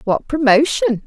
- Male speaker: No, female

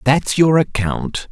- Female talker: No, male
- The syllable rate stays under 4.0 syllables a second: Yes, 3.4 syllables/s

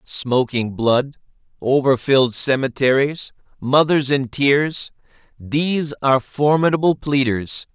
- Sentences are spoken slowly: Yes, slow, 85 wpm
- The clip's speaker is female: No, male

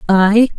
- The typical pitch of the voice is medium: No, high, 210 Hz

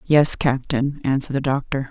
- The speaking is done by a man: No, female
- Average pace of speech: Yes, average, 155 wpm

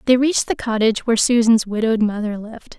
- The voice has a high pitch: Yes, high, 225 Hz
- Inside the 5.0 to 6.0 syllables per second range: No, 6.8 syllables/s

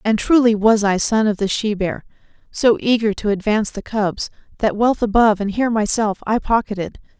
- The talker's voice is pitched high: Yes, high, 215 Hz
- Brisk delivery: No, average, 190 wpm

